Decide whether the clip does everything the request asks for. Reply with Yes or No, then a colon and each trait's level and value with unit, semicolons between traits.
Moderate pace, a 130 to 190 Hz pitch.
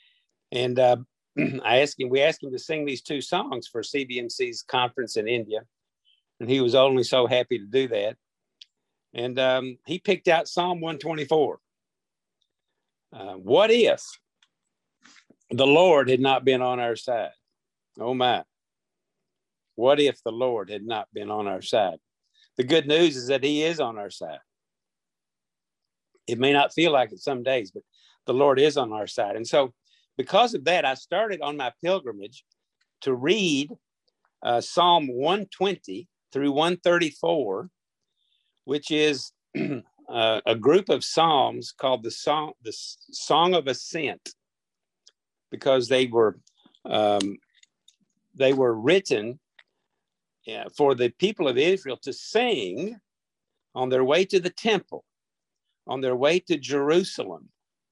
Yes: average, 145 wpm; medium, 140 Hz